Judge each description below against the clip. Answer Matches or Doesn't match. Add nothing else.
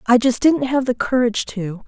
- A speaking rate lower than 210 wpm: Doesn't match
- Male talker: Doesn't match